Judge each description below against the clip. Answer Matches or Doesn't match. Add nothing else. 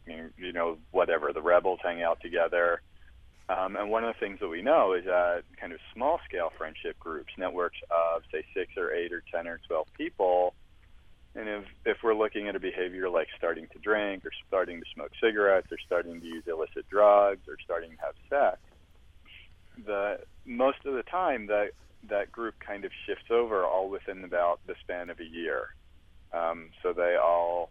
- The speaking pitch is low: Matches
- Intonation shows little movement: Doesn't match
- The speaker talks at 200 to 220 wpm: Doesn't match